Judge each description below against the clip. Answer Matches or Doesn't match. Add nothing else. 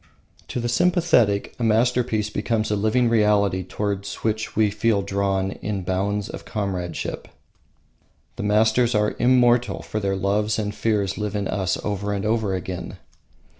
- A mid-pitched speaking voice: Doesn't match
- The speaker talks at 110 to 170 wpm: Matches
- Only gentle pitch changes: Matches